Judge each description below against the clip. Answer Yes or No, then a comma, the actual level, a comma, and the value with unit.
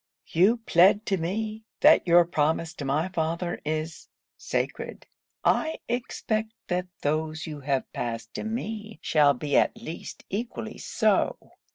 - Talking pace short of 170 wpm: Yes, average, 140 wpm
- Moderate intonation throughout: No, wide, 5.7 semitones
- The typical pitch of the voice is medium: Yes, medium, 170 Hz